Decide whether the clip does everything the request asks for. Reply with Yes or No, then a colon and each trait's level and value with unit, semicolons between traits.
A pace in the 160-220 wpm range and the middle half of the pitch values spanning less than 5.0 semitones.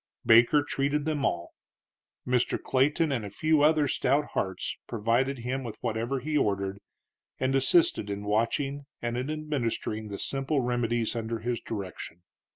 No: average, 150 wpm; average, 4.1 semitones